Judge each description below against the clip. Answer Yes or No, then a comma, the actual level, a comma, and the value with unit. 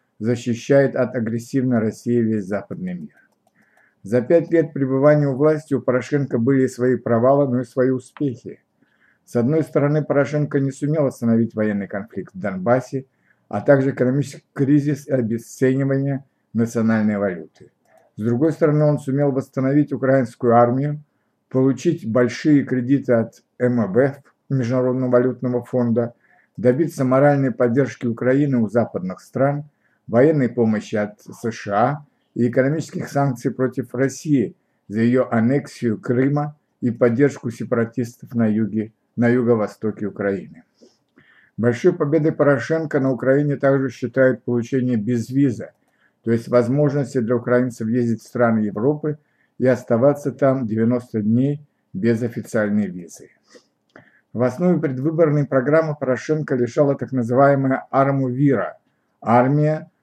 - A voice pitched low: Yes, low, 130 Hz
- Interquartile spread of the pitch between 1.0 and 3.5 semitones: Yes, average, 3.1 semitones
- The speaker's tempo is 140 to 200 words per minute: No, average, 125 wpm